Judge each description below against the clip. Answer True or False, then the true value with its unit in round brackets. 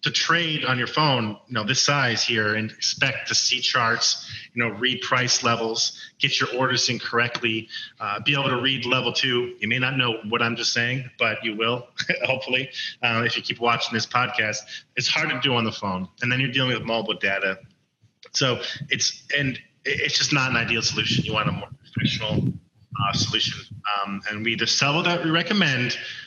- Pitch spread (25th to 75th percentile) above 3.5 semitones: False (2.5 semitones)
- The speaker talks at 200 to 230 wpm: True (205 wpm)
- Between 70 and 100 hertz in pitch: False (120 Hz)